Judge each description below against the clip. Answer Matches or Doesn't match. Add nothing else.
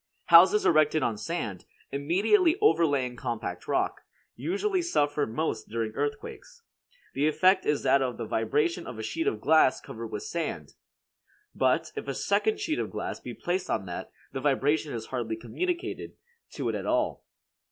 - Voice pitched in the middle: Matches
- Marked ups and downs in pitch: Matches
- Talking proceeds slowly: Doesn't match